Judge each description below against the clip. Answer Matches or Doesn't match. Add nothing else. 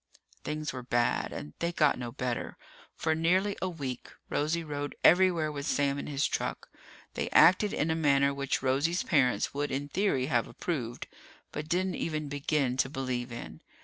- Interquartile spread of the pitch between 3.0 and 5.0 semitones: Matches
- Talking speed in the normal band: Matches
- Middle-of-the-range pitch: Matches